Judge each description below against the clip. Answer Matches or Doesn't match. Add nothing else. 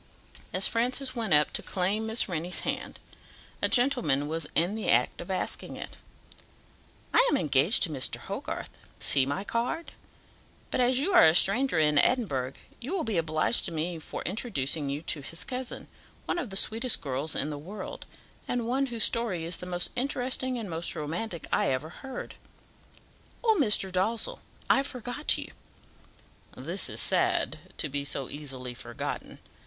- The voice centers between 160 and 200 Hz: Matches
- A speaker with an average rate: Matches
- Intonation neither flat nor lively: Doesn't match